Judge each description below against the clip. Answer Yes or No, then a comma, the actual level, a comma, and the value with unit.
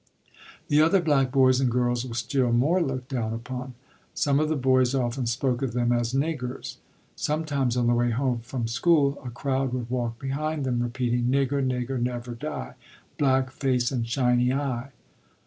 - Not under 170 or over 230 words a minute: Yes, average, 175 wpm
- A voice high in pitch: No, low, 130 Hz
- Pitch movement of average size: No, narrow, 2.2 semitones